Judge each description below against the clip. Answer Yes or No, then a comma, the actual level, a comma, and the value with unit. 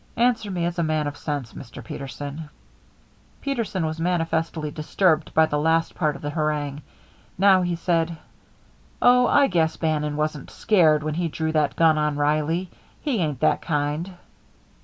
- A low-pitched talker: No, medium, 160 Hz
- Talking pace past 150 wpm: Yes, average, 160 wpm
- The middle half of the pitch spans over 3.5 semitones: No, narrow, 2.6 semitones